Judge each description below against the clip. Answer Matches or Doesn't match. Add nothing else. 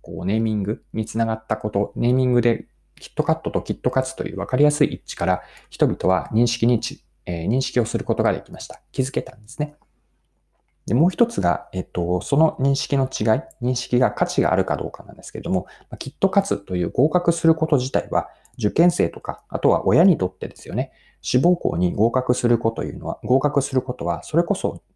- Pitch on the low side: Matches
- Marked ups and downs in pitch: Doesn't match